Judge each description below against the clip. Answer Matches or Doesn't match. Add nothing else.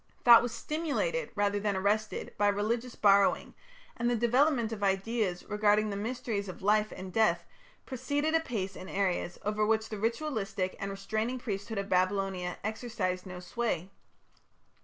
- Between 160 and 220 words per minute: Doesn't match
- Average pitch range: Matches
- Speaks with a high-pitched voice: Matches